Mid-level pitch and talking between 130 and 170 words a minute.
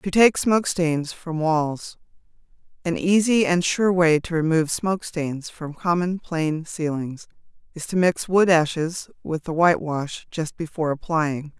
Yes: medium, 165 Hz; average, 150 wpm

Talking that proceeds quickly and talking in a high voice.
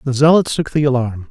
No: fast, 230 wpm; low, 135 Hz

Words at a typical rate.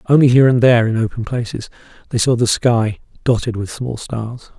Yes: average, 195 wpm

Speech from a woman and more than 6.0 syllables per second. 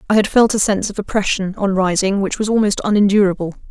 Yes: female; 6.5 syllables/s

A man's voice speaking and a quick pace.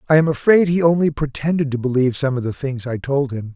Yes: male; fast, 255 wpm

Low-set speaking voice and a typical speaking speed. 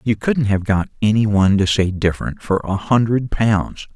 Yes: low, 105 Hz; average, 195 wpm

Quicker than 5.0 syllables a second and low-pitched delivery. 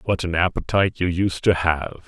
Yes: 5.4 syllables/s; very low, 90 Hz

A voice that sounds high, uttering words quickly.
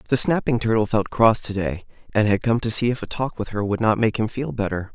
No: low, 110 Hz; fast, 280 wpm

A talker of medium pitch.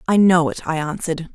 Yes: medium, 165 Hz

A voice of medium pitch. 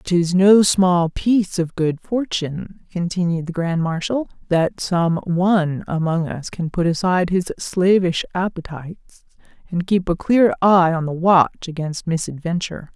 Yes: medium, 175 Hz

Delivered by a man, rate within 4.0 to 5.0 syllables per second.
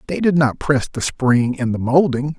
Yes: male; 4.7 syllables/s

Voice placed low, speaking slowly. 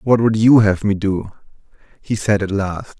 No: low, 105 Hz; average, 200 wpm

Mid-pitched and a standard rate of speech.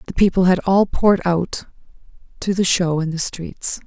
Yes: medium, 180 Hz; average, 185 wpm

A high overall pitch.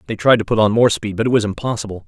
No: low, 110 Hz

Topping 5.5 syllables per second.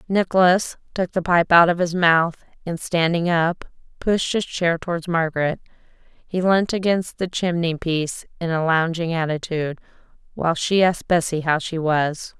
No: 4.8 syllables/s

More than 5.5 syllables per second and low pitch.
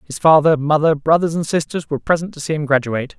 No: 6.5 syllables/s; medium, 155 Hz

